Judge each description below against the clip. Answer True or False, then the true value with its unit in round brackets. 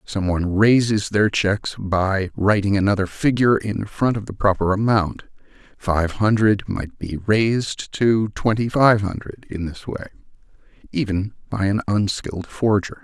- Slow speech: False (145 wpm)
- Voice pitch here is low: True (105 Hz)